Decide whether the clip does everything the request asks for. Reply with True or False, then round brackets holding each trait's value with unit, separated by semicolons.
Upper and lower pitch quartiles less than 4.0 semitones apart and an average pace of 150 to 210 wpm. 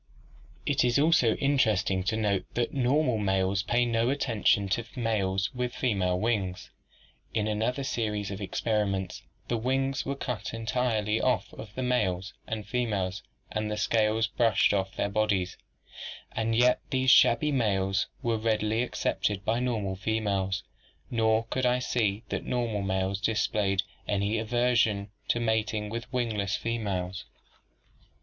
False (3.3 semitones; 140 wpm)